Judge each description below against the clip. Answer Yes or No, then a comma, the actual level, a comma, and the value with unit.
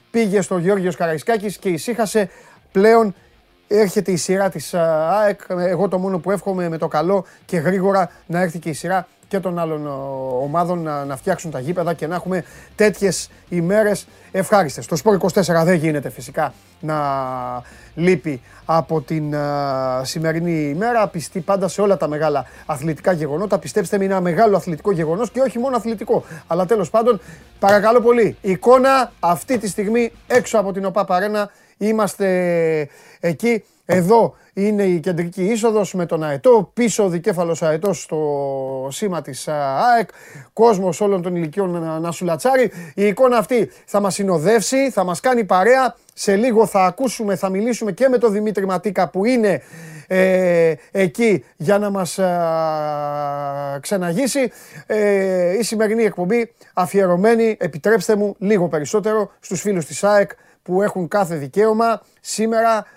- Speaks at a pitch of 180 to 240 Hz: Yes, high, 190 Hz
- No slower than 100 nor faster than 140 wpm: No, average, 150 wpm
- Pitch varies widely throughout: No, average, 4.3 semitones